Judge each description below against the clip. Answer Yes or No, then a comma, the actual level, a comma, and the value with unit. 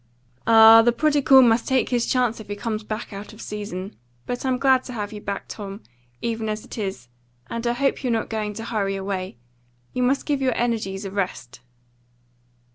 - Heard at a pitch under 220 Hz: No, high, 225 Hz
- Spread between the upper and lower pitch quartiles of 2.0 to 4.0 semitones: Yes, average, 3.2 semitones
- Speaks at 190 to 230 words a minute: Yes, average, 200 wpm